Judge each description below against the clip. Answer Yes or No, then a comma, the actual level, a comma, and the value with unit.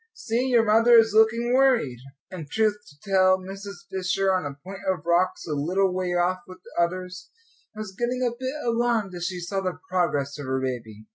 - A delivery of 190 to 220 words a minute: Yes, average, 200 wpm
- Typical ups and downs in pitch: Yes, average, 4.2 semitones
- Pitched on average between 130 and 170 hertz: No, medium, 185 Hz